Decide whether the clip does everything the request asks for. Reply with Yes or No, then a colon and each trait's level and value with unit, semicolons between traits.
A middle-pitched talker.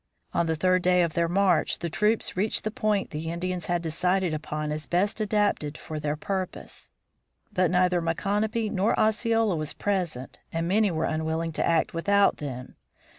Yes: medium, 180 Hz